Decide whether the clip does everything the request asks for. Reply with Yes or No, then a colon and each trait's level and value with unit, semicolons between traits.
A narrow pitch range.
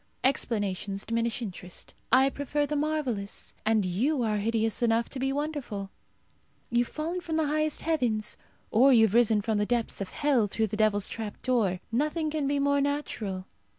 No: average, 5.2 semitones